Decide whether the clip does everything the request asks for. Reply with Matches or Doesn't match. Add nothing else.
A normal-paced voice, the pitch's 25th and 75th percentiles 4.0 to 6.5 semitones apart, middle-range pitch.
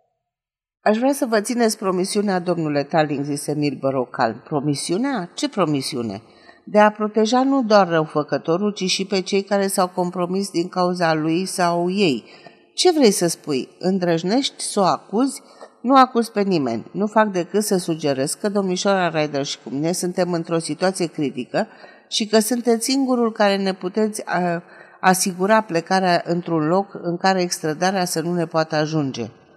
Matches